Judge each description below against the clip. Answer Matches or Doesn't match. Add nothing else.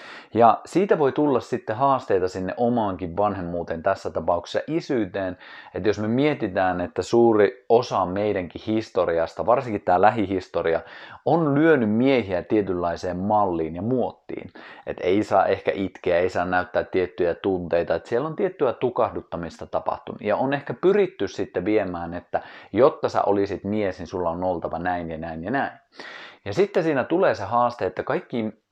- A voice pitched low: Matches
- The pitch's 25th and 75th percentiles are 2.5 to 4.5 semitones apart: Doesn't match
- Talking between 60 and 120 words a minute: Doesn't match